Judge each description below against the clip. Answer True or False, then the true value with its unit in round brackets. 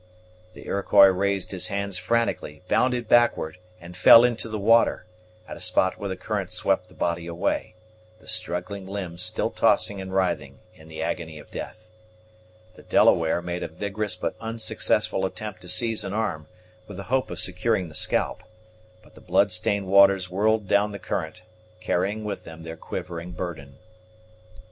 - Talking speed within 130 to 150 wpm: False (165 wpm)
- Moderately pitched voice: False (95 Hz)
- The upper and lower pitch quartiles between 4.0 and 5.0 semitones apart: False (3.2 semitones)